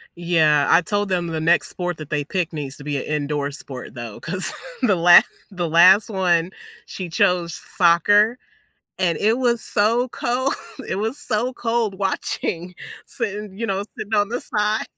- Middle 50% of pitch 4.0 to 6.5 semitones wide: Yes, average, 4.3 semitones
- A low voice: No, medium, 185 Hz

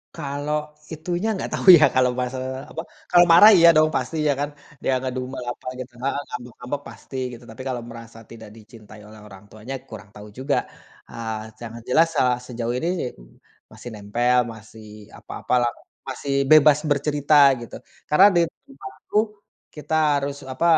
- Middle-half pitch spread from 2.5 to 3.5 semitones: No, average, 4.1 semitones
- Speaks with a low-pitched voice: Yes, low, 130 Hz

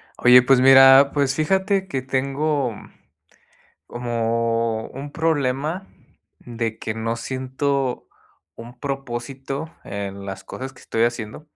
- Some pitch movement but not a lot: Yes, average, 3.2 semitones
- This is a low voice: Yes, low, 130 Hz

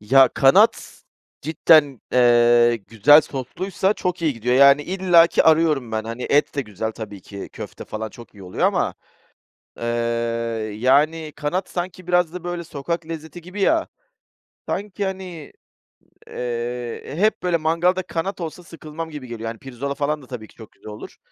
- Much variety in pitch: Yes, wide, 6.3 semitones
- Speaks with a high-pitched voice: No, medium, 150 Hz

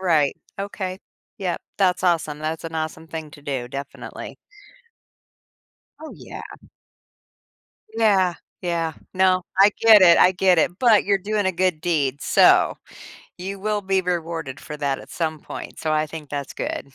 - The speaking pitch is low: No, medium, 170 Hz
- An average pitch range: Yes, average, 3.5 semitones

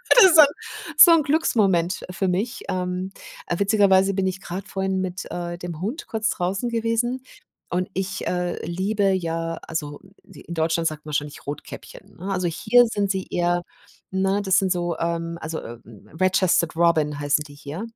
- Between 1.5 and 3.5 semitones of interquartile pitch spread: Yes, average, 2.9 semitones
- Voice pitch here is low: No, medium, 185 Hz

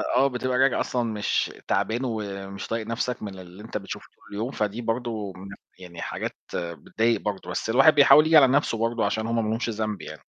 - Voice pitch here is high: No, low, 115 Hz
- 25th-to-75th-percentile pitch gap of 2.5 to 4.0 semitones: Yes, average, 3.1 semitones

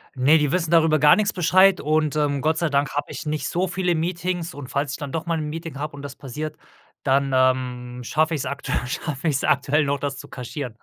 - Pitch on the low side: No, medium, 150 Hz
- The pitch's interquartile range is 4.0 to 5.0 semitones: No, average, 2.9 semitones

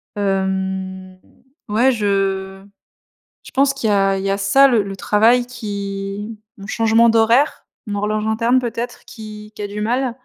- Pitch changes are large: No, average, 2.9 semitones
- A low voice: No, high, 210 Hz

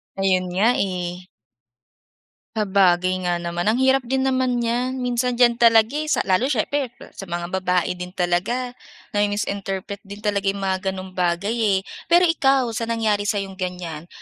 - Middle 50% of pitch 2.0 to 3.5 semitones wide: No, average, 4.7 semitones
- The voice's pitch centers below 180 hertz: No, high, 200 Hz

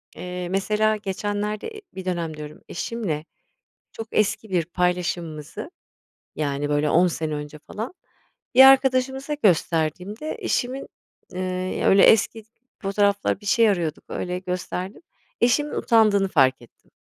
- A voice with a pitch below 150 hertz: No, high, 190 Hz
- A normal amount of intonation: Yes, average, 4.5 semitones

